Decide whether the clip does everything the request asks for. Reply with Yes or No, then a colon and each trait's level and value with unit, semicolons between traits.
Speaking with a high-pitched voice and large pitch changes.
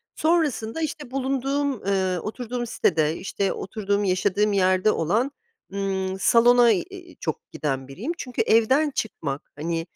Yes: high, 215 Hz; wide, 5.8 semitones